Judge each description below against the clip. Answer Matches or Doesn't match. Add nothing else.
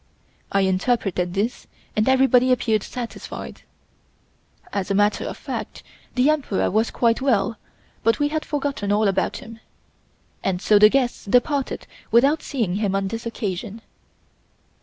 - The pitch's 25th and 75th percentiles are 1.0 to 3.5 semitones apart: Doesn't match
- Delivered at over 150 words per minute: Doesn't match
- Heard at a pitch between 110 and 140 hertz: Doesn't match